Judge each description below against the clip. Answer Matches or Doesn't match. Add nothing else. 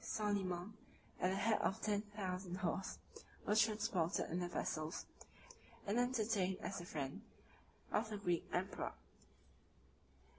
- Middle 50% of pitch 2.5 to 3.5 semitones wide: Matches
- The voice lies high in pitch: Matches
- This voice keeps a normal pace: Doesn't match